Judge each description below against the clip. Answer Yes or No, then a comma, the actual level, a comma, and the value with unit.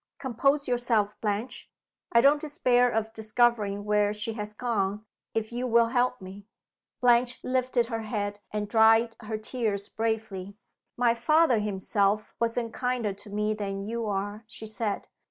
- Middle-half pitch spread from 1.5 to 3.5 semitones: Yes, narrow, 2.6 semitones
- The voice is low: No, high, 220 Hz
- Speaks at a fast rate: No, average, 150 wpm